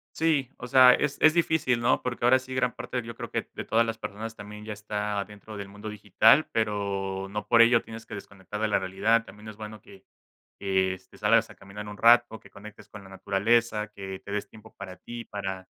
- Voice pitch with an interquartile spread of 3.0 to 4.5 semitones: No, narrow, 2.6 semitones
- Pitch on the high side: No, low, 105 Hz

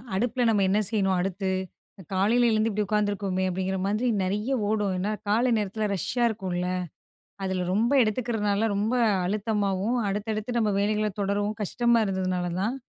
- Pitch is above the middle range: Yes, high, 205 Hz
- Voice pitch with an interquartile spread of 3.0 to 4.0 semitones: No, narrow, 2.4 semitones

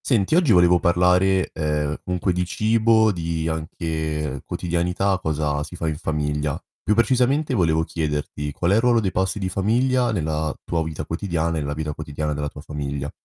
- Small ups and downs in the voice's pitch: No, average, 4.2 semitones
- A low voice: Yes, very low, 85 Hz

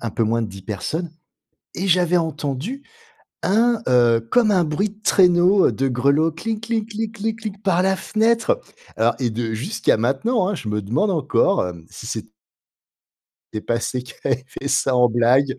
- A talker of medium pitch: Yes, medium, 155 Hz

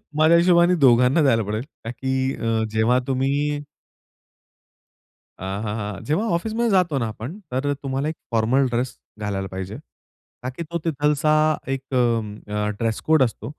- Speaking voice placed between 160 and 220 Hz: No, low, 130 Hz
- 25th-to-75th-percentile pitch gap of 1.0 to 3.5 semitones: No, average, 5.3 semitones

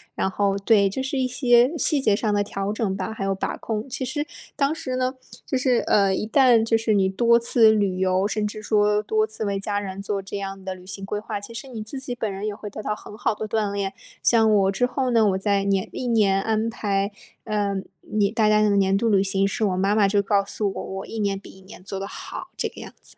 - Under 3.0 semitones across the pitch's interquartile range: Yes, narrow, 2.5 semitones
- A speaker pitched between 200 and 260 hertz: Yes, high, 210 Hz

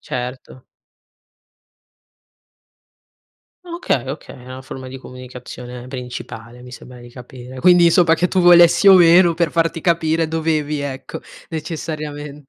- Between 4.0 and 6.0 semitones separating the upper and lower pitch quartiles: Yes, average, 4.7 semitones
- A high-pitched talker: No, medium, 150 Hz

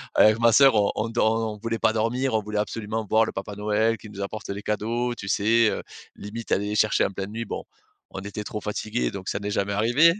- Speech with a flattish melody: Yes, narrow, 1.8 semitones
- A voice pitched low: Yes, low, 110 Hz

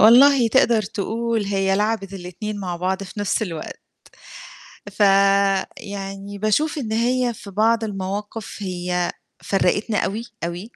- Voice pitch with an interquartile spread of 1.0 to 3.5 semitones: Yes, narrow, 2.5 semitones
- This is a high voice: Yes, high, 205 Hz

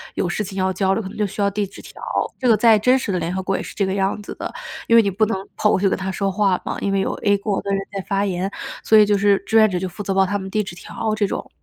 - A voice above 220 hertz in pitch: No, high, 200 Hz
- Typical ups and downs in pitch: No, narrow, 1.7 semitones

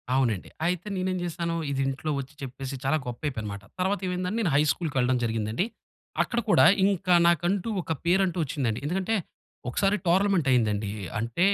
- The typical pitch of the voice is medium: Yes, medium, 155 Hz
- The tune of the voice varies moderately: No, wide, 6.5 semitones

